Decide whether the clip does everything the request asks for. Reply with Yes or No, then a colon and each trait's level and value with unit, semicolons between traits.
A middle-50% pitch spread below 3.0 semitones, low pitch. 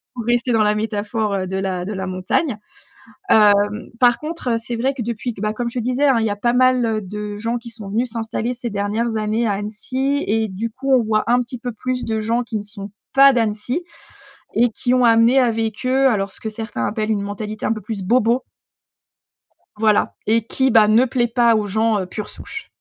No: narrow, 2.6 semitones; high, 225 Hz